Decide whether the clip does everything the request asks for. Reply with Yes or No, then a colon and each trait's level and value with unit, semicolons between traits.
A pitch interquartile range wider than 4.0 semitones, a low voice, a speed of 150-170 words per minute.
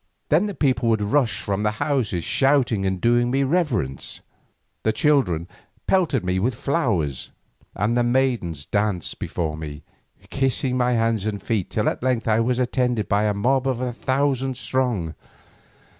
Yes: average, 4.4 semitones; low, 120 Hz; average, 160 wpm